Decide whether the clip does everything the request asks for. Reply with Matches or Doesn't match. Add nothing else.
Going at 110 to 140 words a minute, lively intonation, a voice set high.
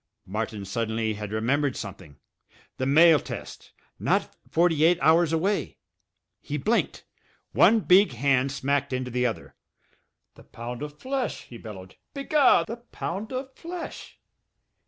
Doesn't match